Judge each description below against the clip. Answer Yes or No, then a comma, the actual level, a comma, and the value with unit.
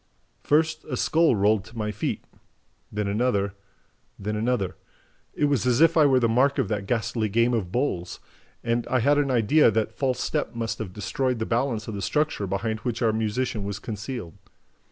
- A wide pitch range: No, average, 3.6 semitones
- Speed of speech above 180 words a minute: Yes, average, 190 wpm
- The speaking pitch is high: No, low, 115 Hz